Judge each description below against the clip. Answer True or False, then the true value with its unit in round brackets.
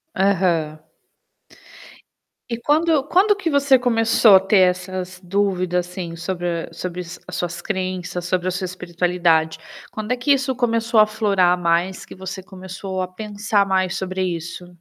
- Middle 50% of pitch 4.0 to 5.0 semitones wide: False (3.3 semitones)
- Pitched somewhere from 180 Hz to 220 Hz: True (185 Hz)